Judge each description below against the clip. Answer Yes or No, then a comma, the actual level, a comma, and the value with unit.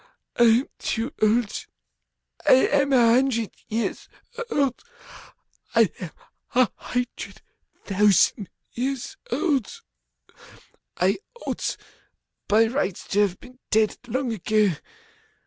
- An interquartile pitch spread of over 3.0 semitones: Yes, average, 3.4 semitones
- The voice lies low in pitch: No, high, 230 Hz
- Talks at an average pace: No, slow, 105 wpm